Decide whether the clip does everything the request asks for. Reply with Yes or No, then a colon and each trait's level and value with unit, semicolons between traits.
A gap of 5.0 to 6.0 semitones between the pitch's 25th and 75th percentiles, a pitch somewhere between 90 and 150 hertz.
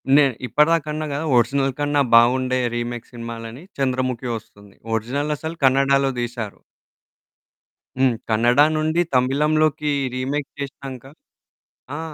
No: average, 3.4 semitones; low, 135 Hz